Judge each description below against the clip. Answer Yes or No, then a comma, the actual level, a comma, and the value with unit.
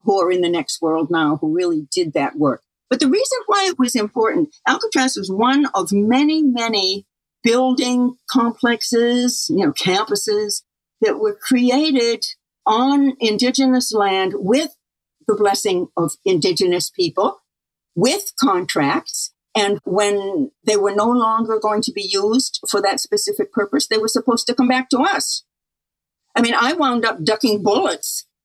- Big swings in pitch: Yes, wide, 6.4 semitones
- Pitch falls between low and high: No, very high, 250 Hz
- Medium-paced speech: Yes, average, 155 wpm